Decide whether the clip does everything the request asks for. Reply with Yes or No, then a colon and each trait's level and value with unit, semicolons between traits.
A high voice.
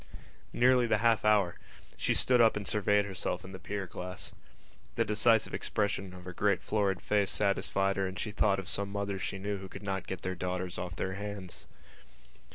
No: low, 100 Hz